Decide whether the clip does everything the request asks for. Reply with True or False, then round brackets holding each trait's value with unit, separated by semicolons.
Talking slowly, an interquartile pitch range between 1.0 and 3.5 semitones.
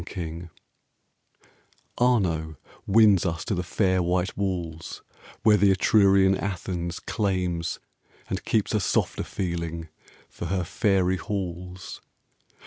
True (110 wpm; 2.4 semitones)